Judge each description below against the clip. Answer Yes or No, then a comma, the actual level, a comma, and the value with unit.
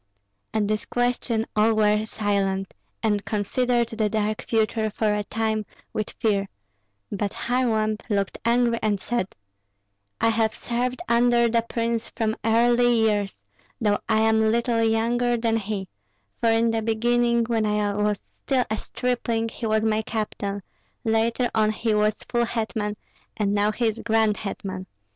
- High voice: Yes, high, 220 Hz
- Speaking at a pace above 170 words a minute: No, average, 155 wpm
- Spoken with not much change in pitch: Yes, narrow, 1.9 semitones